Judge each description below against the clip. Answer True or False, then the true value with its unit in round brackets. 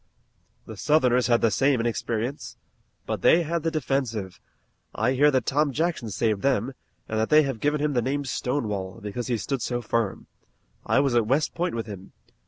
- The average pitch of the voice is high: False (125 Hz)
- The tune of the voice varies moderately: True (4.3 semitones)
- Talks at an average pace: True (190 wpm)